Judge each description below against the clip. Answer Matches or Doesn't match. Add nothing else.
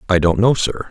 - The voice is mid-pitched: Doesn't match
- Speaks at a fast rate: Matches